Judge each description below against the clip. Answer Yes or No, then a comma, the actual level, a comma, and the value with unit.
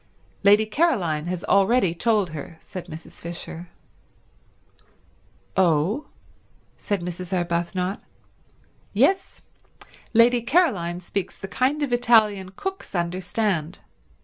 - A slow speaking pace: Yes, slow, 95 wpm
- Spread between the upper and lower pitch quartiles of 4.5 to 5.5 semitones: Yes, average, 5.2 semitones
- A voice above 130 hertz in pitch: Yes, high, 190 Hz